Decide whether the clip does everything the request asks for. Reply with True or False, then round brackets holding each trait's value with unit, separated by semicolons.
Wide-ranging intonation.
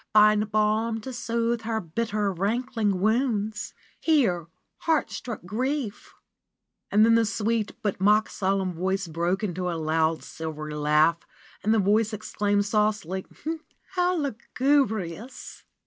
False (3.6 semitones)